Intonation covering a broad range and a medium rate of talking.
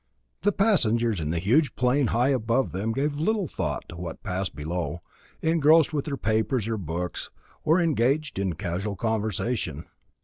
Yes: wide, 7.6 semitones; average, 160 wpm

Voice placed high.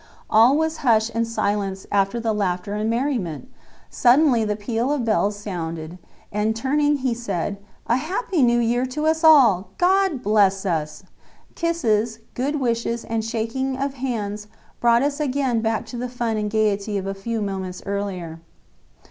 Yes: high, 225 Hz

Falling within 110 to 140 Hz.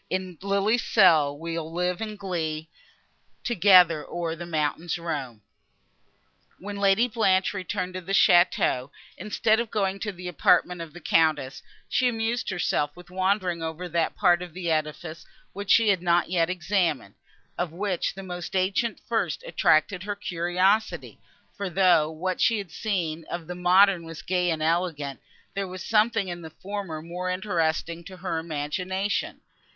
No: medium, 180 Hz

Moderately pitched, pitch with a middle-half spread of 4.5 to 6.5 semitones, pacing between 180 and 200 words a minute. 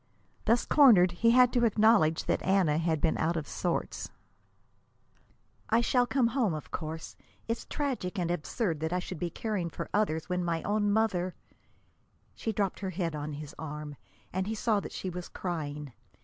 Yes: medium, 180 Hz; wide, 5.4 semitones; average, 185 wpm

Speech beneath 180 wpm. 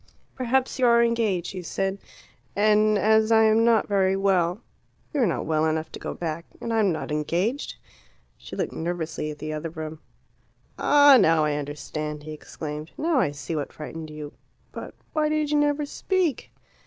No: average, 185 wpm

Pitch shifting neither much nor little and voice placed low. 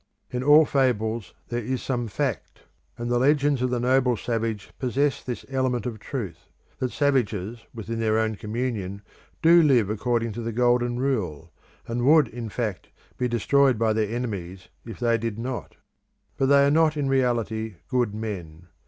Yes: average, 3.0 semitones; low, 120 Hz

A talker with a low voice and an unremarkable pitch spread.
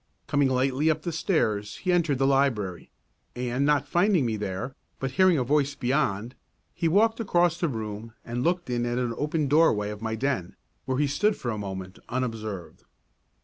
No: low, 130 Hz; wide, 5.8 semitones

